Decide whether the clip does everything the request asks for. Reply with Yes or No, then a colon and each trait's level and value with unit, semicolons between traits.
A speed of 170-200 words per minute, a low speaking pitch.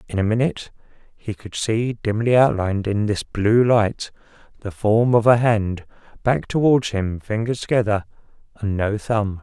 No: average, 160 wpm; low, 110 Hz